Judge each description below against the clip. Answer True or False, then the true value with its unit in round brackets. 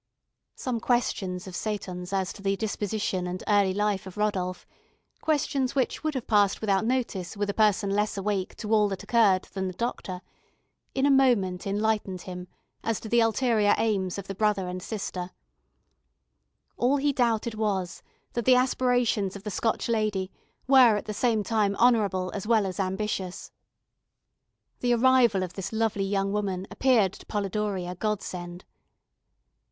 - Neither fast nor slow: True (160 wpm)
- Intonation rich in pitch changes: False (3.2 semitones)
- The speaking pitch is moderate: False (205 Hz)